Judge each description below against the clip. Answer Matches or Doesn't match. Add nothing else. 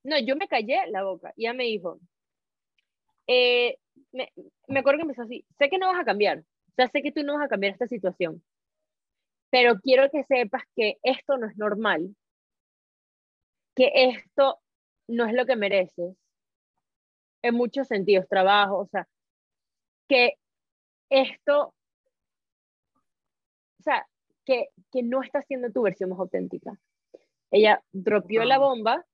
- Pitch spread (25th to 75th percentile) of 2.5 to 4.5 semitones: Doesn't match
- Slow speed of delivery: Doesn't match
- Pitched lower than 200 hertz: Doesn't match